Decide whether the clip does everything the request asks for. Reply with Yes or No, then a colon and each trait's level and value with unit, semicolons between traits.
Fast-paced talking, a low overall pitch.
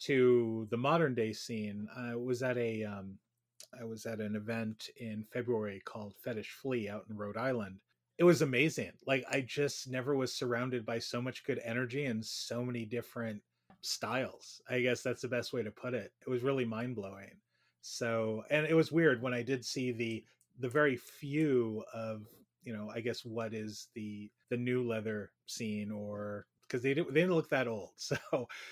No: average, 190 wpm; low, 120 Hz